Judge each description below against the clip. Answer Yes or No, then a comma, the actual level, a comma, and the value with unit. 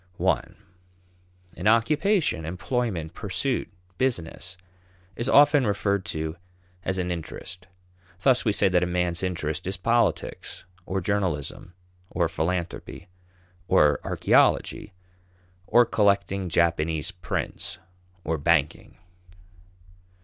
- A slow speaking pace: Yes, slow, 100 wpm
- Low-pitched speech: Yes, very low, 90 Hz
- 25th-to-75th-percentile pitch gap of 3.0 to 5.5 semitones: Yes, average, 4.2 semitones